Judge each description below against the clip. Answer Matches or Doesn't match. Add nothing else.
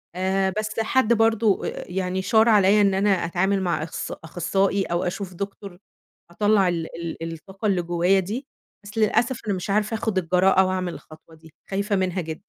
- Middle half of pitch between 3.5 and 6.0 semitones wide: Doesn't match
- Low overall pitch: Doesn't match